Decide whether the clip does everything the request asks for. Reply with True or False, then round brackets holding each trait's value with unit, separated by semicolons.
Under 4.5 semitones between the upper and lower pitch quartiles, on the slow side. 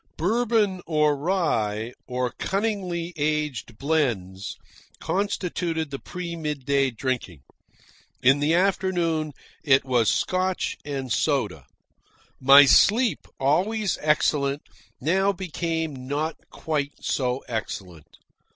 False (5.2 semitones; 100 wpm)